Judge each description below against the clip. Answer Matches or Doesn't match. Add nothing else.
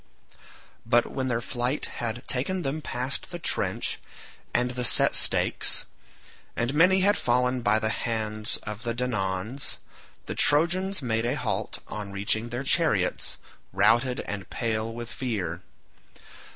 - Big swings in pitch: Doesn't match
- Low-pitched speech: Matches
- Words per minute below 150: Matches